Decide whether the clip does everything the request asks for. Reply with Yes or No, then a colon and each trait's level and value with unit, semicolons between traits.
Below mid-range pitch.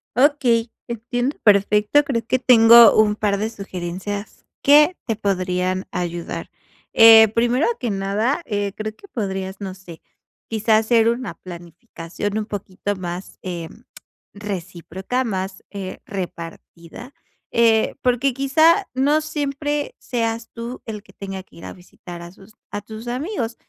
No: high, 215 Hz